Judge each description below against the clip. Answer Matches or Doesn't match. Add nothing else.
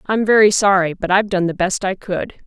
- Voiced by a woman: Matches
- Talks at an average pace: Doesn't match